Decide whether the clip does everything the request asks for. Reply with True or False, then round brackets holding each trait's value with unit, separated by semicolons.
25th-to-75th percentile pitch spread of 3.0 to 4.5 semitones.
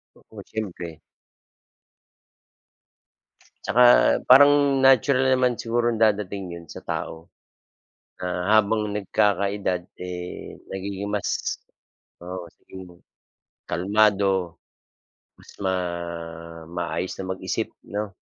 True (3.4 semitones)